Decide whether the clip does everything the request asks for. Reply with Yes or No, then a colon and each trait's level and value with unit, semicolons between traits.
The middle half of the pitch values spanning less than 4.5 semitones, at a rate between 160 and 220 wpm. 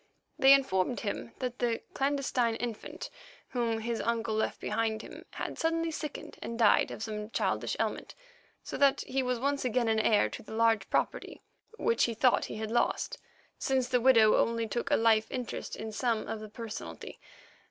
Yes: average, 2.7 semitones; average, 175 wpm